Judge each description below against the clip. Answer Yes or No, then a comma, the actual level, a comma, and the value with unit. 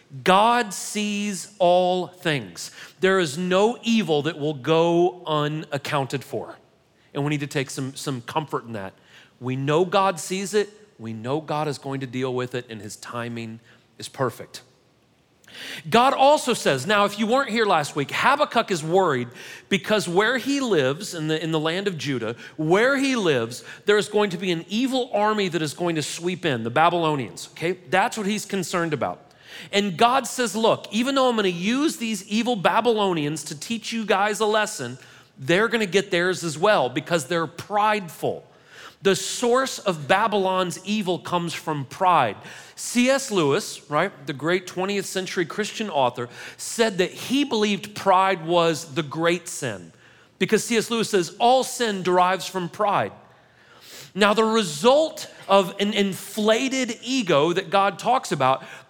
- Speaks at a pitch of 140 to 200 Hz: Yes, medium, 185 Hz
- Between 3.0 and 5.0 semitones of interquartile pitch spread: No, wide, 5.6 semitones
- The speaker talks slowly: No, average, 165 wpm